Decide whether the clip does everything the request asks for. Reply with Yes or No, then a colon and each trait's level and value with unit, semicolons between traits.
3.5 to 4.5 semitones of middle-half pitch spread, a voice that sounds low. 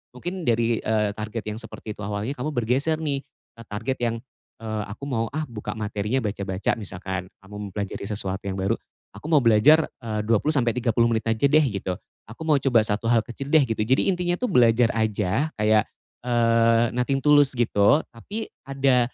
Yes: average, 4.0 semitones; low, 115 Hz